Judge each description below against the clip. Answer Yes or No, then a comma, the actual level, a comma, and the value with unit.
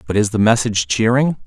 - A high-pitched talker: No, low, 110 Hz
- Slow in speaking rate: No, fast, 205 wpm